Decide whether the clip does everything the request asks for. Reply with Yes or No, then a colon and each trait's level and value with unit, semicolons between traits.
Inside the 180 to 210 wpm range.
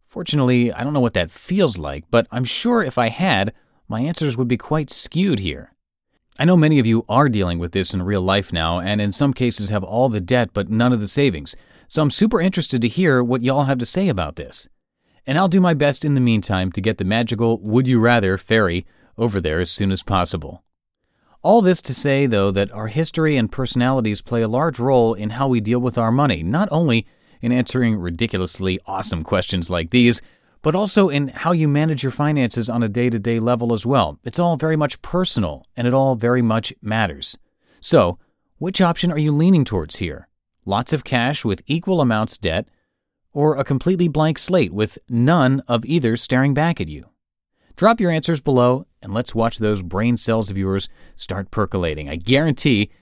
Yes: fast, 205 wpm